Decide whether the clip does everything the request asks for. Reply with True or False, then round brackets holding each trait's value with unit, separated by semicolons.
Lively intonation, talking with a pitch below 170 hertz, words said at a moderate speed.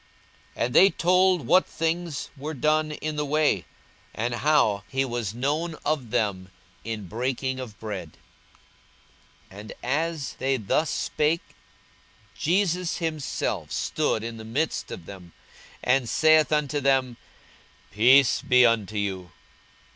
False (5.7 semitones; 135 Hz; 130 wpm)